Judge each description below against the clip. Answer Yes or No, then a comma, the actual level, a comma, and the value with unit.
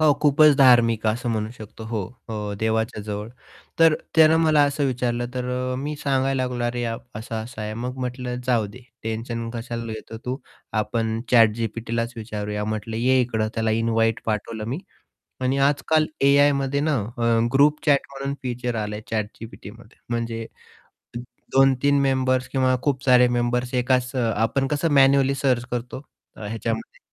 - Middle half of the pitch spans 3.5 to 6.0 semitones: No, average, 3.1 semitones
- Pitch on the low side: Yes, low, 120 Hz